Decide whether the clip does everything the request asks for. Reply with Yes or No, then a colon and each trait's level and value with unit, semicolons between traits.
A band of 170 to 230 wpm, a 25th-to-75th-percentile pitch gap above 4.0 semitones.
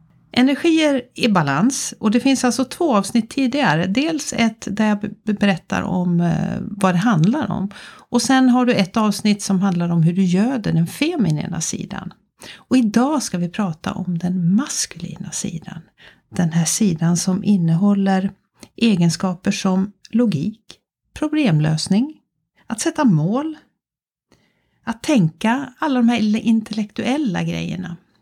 No: average, 135 wpm; average, 5.0 semitones